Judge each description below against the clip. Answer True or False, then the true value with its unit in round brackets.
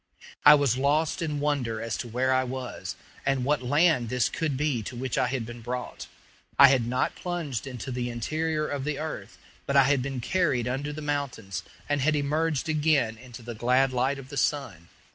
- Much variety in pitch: False (3.2 semitones)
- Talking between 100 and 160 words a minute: False (200 wpm)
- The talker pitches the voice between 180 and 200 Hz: False (135 Hz)